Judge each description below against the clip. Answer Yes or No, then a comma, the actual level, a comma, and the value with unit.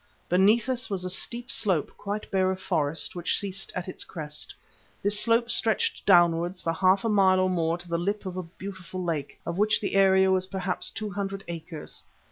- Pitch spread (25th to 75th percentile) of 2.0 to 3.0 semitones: Yes, narrow, 2.5 semitones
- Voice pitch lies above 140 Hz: Yes, medium, 185 Hz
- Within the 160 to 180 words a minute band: No, average, 200 wpm